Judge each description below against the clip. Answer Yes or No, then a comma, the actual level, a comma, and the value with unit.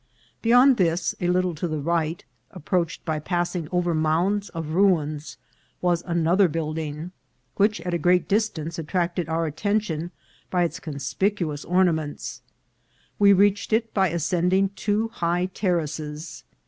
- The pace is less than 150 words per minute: Yes, average, 140 wpm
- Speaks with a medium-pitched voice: Yes, medium, 175 Hz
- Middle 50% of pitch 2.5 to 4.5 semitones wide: Yes, average, 3.1 semitones